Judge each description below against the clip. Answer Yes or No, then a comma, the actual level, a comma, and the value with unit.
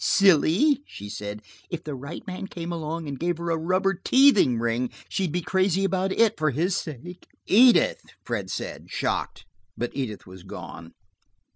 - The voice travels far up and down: Yes, wide, 6.4 semitones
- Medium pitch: Yes, medium, 170 Hz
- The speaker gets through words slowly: No, average, 165 wpm